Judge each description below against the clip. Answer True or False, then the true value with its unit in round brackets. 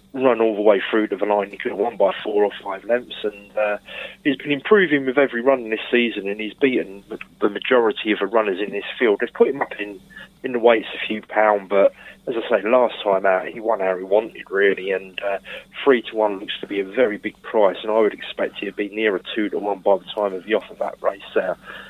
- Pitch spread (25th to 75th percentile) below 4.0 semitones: True (2.9 semitones)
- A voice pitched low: True (110 Hz)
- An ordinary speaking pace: False (265 wpm)